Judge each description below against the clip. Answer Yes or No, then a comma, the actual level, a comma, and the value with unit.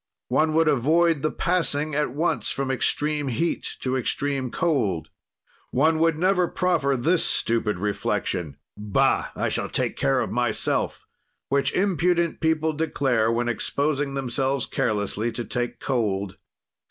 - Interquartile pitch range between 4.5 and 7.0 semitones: Yes, average, 5.2 semitones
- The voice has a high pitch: No, medium, 140 Hz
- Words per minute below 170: Yes, slow, 135 wpm